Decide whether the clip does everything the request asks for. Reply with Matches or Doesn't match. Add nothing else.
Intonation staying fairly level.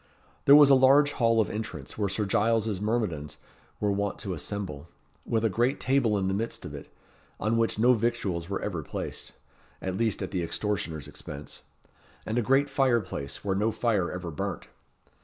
Doesn't match